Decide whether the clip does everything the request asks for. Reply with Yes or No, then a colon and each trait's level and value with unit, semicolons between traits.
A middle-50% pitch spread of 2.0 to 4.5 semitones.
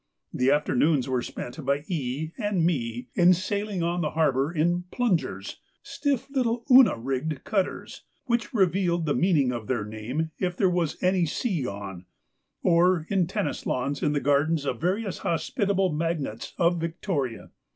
No: average, 5.3 semitones